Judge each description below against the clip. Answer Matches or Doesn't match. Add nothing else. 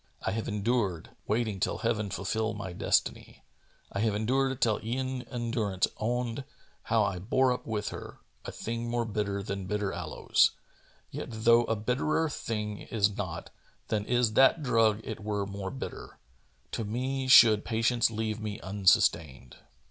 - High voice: Doesn't match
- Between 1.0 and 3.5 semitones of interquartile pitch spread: Matches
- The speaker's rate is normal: Matches